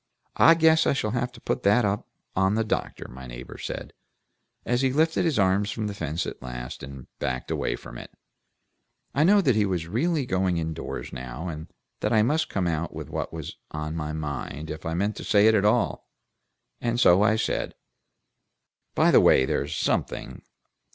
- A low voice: Yes, very low, 95 Hz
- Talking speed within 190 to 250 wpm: Yes, average, 200 wpm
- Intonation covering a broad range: Yes, wide, 7.4 semitones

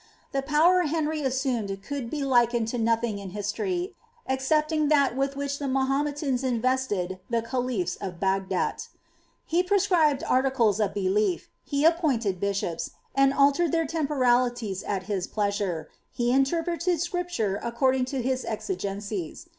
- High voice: Yes, very high, 255 Hz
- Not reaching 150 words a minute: Yes, average, 140 wpm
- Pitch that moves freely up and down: Yes, wide, 5.8 semitones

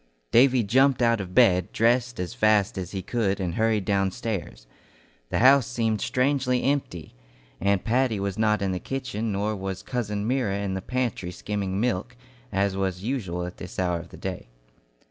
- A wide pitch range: No, average, 4.4 semitones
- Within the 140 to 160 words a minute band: No, average, 175 wpm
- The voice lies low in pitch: Yes, low, 105 Hz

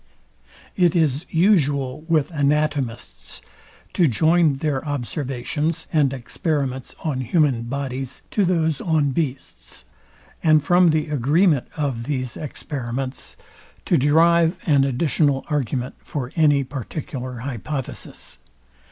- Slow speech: Yes, slow, 110 wpm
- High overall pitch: No, medium, 145 Hz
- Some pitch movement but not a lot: Yes, average, 3.3 semitones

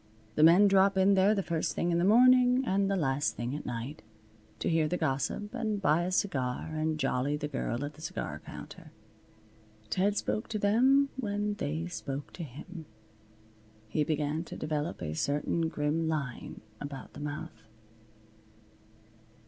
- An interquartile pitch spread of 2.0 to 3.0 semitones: No, average, 5.3 semitones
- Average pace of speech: Yes, average, 165 wpm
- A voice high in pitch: No, medium, 160 Hz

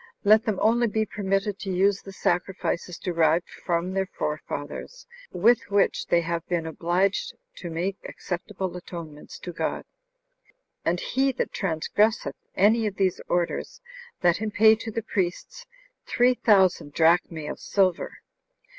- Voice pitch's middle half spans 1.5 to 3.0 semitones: No, average, 3.6 semitones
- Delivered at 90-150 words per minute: Yes, average, 140 wpm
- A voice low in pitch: No, high, 190 Hz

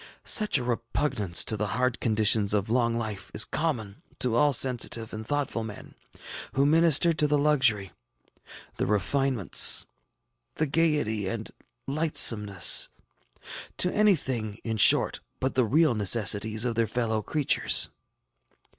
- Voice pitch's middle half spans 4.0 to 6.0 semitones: Yes, average, 5.0 semitones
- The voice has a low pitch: Yes, low, 115 Hz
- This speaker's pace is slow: Yes, slow, 130 wpm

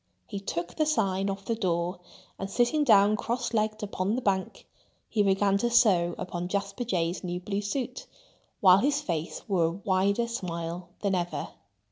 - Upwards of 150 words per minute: Yes, average, 170 wpm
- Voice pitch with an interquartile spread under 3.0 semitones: No, average, 3.5 semitones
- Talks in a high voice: Yes, high, 195 Hz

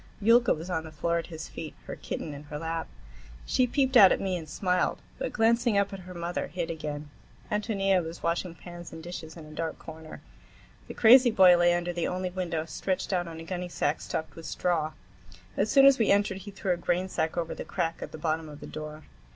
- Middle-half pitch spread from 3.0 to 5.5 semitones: Yes, average, 3.3 semitones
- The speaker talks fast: Yes, fast, 220 wpm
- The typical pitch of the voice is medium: Yes, medium, 175 Hz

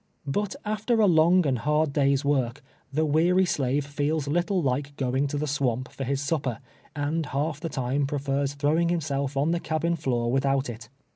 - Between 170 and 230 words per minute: Yes, average, 195 wpm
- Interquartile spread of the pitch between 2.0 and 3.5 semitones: Yes, average, 2.7 semitones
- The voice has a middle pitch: Yes, medium, 145 Hz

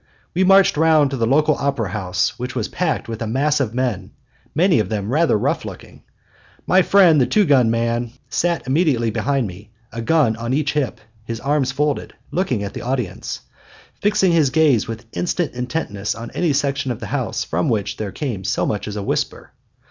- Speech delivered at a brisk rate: No, average, 195 wpm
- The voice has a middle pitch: No, low, 130 Hz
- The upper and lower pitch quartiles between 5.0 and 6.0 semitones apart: Yes, wide, 5.4 semitones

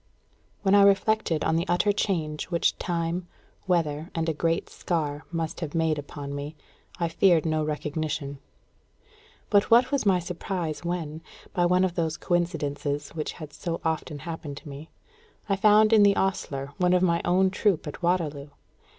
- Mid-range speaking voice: Yes, medium, 165 Hz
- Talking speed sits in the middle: Yes, average, 170 wpm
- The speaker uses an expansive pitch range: No, average, 3.3 semitones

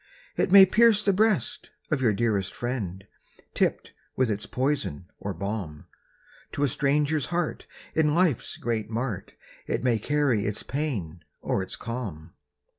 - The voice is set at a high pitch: No, low, 125 Hz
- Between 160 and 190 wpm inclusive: No, average, 145 wpm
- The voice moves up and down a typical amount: No, wide, 6.8 semitones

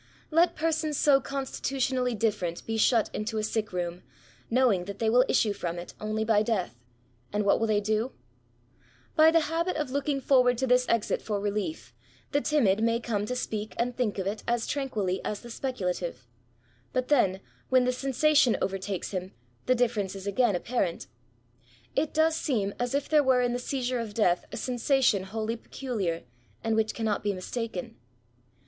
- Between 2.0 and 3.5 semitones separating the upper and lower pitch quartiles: No, average, 4.1 semitones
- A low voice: No, high, 230 Hz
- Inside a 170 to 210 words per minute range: Yes, average, 180 wpm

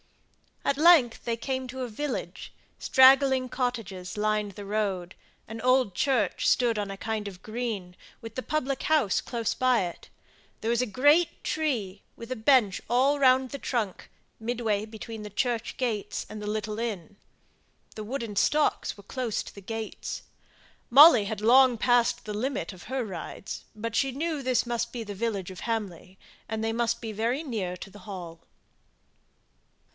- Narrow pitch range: No, average, 3.7 semitones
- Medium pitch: No, high, 230 Hz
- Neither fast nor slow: Yes, average, 170 wpm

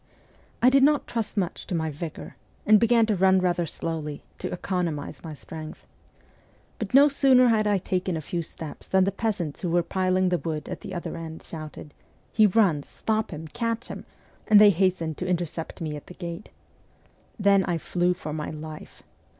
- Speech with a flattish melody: No, average, 4.4 semitones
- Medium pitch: Yes, medium, 180 Hz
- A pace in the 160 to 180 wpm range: No, average, 195 wpm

